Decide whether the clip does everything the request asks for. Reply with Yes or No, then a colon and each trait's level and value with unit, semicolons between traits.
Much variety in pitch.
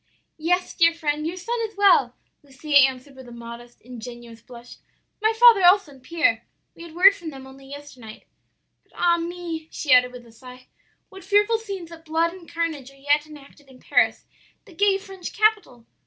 Yes: wide, 5.8 semitones